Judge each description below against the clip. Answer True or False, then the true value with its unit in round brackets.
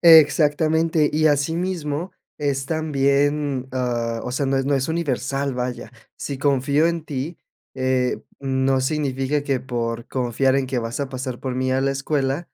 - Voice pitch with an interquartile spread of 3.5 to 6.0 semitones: False (2.4 semitones)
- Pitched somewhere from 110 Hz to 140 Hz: True (135 Hz)